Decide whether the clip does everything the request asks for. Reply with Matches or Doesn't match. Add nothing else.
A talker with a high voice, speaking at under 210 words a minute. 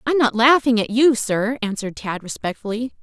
Matches